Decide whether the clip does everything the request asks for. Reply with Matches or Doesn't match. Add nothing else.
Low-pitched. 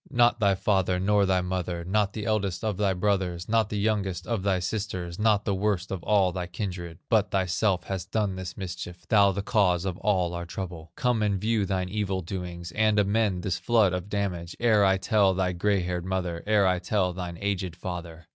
Matches